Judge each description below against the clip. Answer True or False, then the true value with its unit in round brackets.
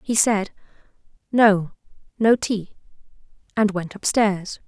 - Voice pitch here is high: True (205 Hz)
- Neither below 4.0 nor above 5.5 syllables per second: False (3.6 syllables/s)